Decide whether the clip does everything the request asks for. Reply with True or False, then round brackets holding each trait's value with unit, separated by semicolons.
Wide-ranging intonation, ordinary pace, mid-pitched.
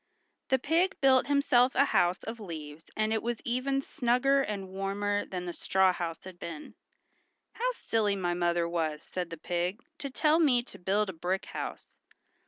False (6.4 semitones; 180 wpm; 205 Hz)